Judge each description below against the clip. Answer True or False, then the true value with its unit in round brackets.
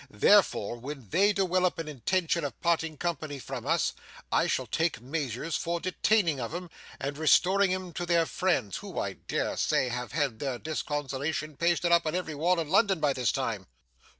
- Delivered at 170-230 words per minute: True (180 wpm)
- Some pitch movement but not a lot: True (3.9 semitones)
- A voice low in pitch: False (160 Hz)